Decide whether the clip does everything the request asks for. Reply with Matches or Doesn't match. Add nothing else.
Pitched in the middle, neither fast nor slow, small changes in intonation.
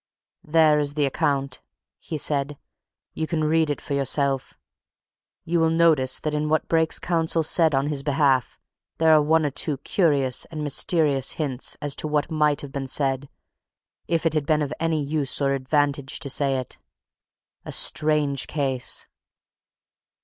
Matches